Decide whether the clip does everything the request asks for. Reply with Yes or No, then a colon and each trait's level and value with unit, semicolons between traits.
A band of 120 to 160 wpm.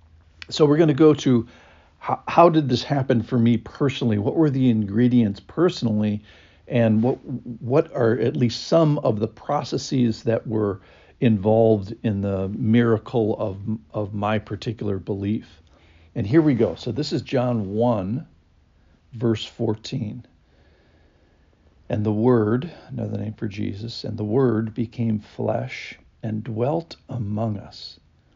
Yes: average, 140 wpm